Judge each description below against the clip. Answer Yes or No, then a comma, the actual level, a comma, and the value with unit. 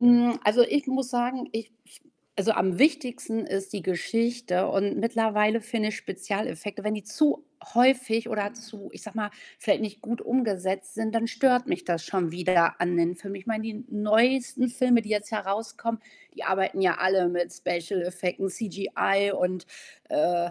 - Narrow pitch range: No, average, 3.9 semitones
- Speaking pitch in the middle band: No, high, 215 Hz